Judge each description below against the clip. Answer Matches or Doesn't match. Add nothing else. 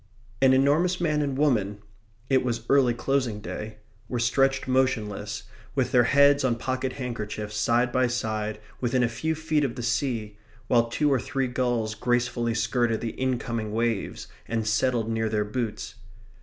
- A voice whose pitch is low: Matches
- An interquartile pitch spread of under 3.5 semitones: Matches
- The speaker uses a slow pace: Doesn't match